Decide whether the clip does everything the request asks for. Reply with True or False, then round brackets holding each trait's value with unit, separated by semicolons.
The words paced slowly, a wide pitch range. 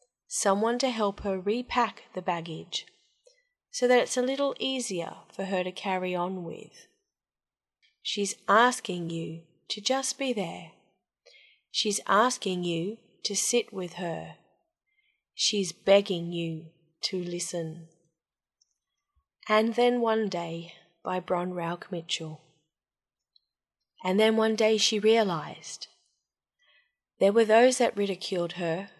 False (120 wpm; 4.7 semitones)